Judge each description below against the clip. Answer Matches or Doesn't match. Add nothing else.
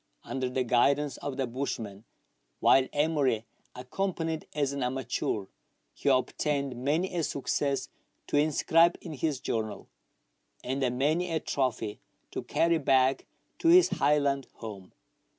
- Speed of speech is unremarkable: Doesn't match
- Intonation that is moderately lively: Matches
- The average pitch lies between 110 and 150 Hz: Matches